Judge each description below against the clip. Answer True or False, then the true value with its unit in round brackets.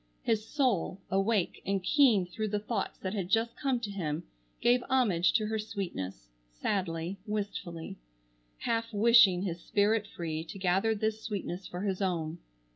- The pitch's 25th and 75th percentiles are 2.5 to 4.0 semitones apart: True (3.7 semitones)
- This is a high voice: True (200 Hz)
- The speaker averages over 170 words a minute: False (155 wpm)